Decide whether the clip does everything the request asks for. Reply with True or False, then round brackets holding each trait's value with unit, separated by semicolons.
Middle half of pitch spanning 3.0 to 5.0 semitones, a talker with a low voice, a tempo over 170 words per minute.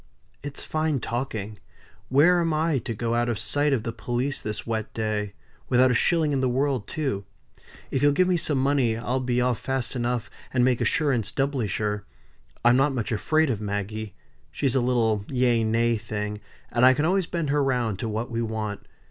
True (3.9 semitones; 125 Hz; 200 wpm)